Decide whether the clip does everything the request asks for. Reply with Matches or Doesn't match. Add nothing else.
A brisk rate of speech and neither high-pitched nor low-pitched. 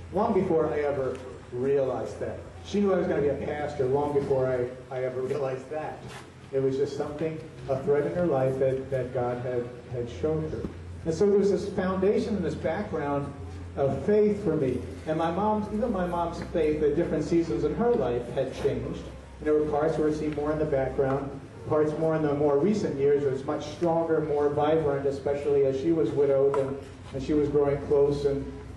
Matches